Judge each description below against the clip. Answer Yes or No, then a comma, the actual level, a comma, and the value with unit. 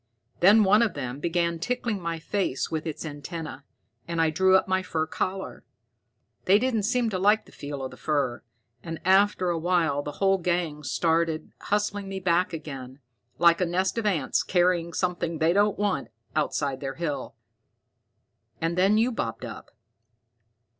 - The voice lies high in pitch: No, medium, 170 Hz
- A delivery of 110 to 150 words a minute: No, average, 165 wpm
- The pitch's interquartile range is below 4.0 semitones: Yes, average, 3.6 semitones